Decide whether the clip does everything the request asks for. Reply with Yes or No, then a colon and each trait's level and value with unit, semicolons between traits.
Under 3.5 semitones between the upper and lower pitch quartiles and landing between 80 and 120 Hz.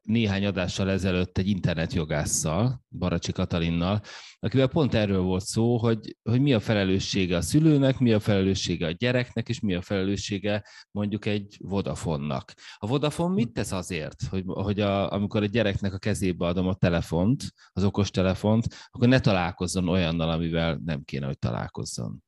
No: average, 3.8 semitones; low, 100 Hz